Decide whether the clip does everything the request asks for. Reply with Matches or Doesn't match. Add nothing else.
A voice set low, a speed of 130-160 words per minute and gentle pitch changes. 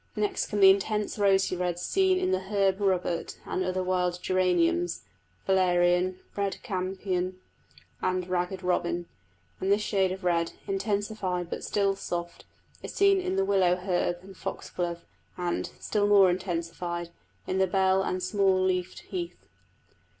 Doesn't match